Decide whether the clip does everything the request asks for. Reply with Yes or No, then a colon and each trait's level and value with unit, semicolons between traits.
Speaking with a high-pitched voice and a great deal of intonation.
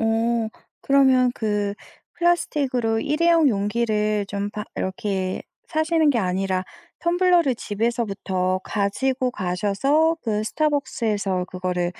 Yes: high, 225 Hz; wide, 5.7 semitones